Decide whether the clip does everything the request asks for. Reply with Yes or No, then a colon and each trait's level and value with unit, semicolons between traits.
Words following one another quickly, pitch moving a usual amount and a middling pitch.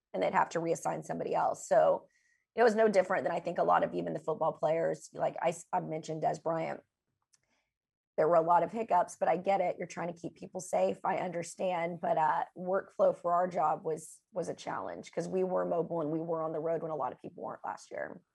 No: fast, 240 wpm; narrow, 2.2 semitones; medium, 175 Hz